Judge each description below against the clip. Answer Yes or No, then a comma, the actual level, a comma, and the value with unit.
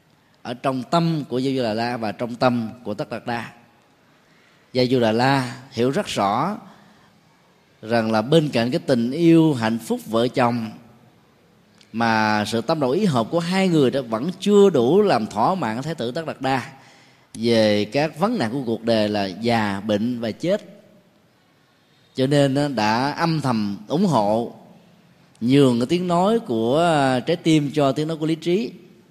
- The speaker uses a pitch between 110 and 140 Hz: Yes, low, 135 Hz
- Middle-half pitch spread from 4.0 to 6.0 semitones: No, wide, 6.4 semitones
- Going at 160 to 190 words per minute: Yes, average, 175 wpm